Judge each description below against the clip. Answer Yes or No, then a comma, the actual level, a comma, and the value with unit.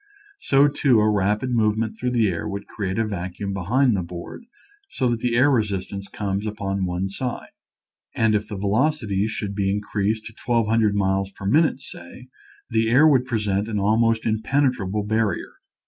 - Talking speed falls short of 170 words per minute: No, average, 175 wpm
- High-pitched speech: No, low, 105 Hz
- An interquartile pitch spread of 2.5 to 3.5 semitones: Yes, average, 3.1 semitones